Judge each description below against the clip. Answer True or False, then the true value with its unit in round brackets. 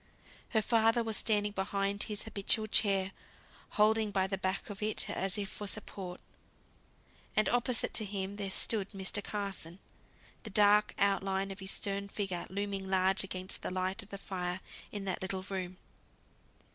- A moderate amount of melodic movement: False (1.6 semitones)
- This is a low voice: False (200 Hz)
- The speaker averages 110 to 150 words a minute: False (165 wpm)